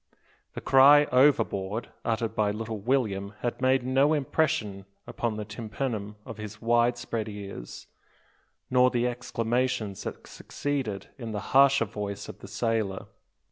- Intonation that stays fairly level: No, average, 3.6 semitones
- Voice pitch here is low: Yes, low, 115 Hz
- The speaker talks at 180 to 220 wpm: No, average, 140 wpm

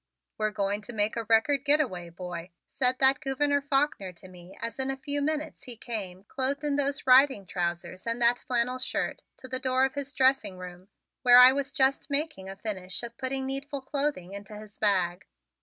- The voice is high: Yes, very high, 250 Hz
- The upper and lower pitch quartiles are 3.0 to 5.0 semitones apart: No, wide, 5.6 semitones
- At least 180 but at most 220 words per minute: Yes, average, 200 wpm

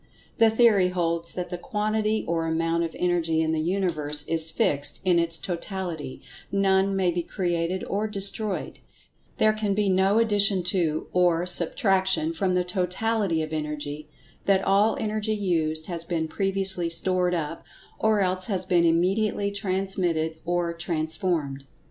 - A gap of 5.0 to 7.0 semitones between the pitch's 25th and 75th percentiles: No, average, 3.0 semitones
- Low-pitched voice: No, medium, 180 Hz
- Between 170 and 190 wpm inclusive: No, average, 140 wpm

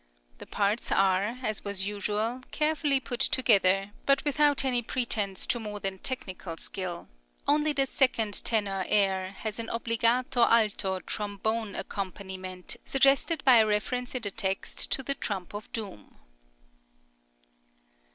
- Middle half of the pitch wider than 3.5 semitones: Yes, average, 4.4 semitones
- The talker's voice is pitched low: No, high, 215 Hz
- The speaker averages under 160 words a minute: Yes, slow, 135 wpm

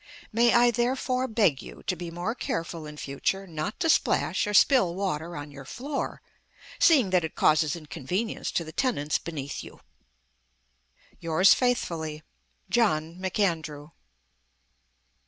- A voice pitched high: No, medium, 175 Hz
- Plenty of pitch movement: Yes, wide, 6.7 semitones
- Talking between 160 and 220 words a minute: No, slow, 135 wpm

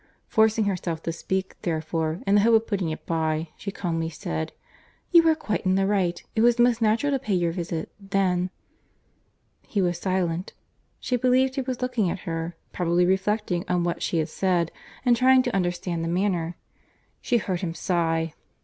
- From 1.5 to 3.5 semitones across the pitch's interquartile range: No, average, 4.5 semitones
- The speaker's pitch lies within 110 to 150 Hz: No, medium, 185 Hz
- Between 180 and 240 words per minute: Yes, average, 185 wpm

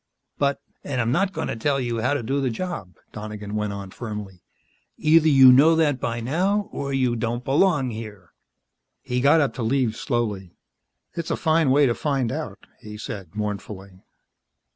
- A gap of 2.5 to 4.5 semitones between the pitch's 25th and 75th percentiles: No, average, 5.2 semitones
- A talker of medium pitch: No, low, 125 Hz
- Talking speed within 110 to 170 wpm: No, average, 185 wpm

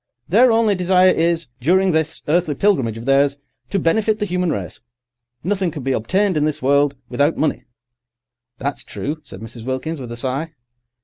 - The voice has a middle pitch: Yes, medium, 160 Hz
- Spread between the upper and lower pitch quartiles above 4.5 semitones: Yes, average, 5.2 semitones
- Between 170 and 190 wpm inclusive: Yes, average, 175 wpm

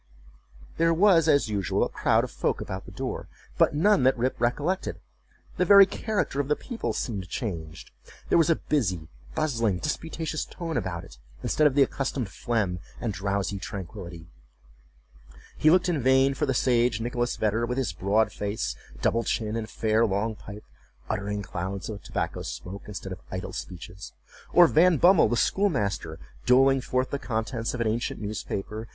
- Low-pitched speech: Yes, low, 115 Hz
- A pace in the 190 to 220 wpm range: No, average, 170 wpm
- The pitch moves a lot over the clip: Yes, wide, 6.3 semitones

